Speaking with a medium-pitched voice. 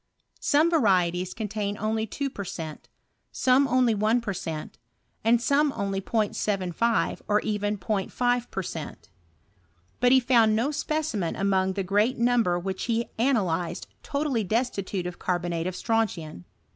No: high, 215 Hz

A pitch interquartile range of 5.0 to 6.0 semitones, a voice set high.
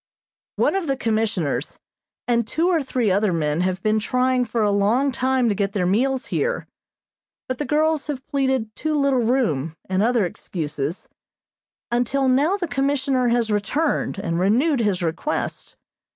Yes: wide, 5.4 semitones; high, 240 Hz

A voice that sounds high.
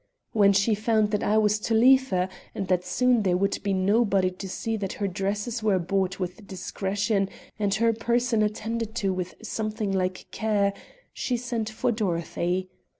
Yes: high, 205 Hz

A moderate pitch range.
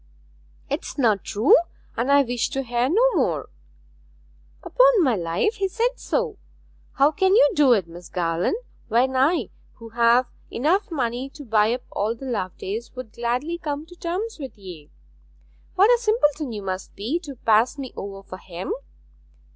No: wide, 7.1 semitones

